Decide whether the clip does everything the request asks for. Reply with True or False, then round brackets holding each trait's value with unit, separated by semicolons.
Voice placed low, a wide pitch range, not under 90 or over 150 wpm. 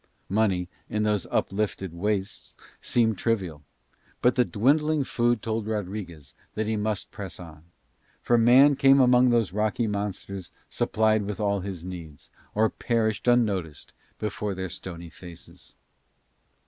False (105 Hz; 3.5 semitones; 135 wpm)